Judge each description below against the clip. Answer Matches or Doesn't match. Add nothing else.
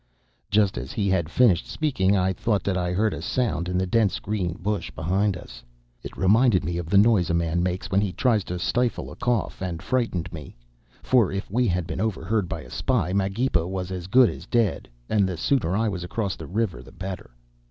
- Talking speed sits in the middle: Doesn't match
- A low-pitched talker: Matches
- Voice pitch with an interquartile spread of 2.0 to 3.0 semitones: Doesn't match